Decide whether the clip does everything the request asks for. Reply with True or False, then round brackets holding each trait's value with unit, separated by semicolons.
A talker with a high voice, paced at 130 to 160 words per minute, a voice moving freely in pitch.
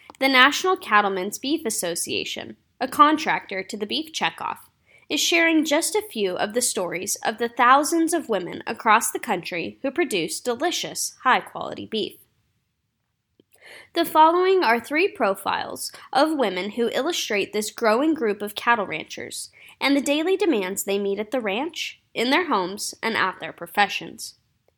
True (255 Hz; 155 wpm; 7.6 semitones)